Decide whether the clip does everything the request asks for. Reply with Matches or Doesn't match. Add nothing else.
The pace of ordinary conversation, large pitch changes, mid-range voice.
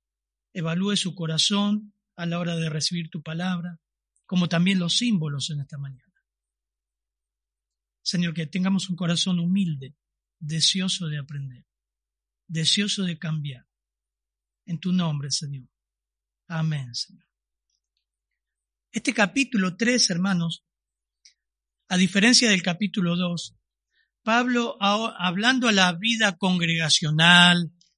Doesn't match